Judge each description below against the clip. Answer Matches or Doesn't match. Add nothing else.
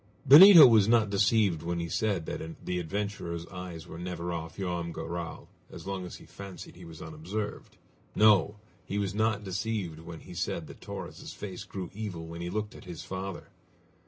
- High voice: Doesn't match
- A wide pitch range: Doesn't match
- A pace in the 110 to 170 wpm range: Doesn't match